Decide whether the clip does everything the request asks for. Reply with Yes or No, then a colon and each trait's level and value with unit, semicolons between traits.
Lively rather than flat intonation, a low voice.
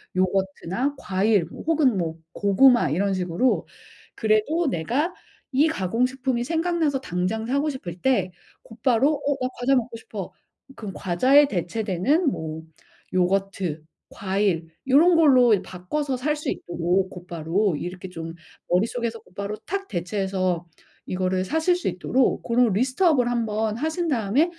No: wide, 6.4 semitones; high, 220 Hz